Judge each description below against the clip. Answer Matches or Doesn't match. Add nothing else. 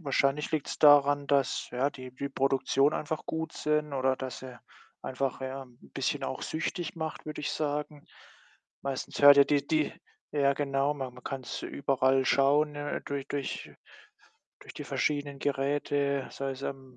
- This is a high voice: Doesn't match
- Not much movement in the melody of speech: Matches